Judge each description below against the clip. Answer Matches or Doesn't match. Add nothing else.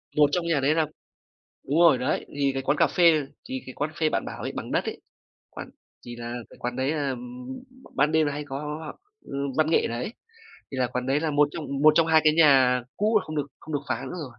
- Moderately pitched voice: Matches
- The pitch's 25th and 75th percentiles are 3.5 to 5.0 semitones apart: Doesn't match